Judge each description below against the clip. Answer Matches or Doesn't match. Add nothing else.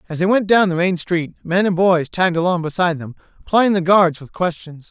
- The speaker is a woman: Doesn't match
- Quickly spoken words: Matches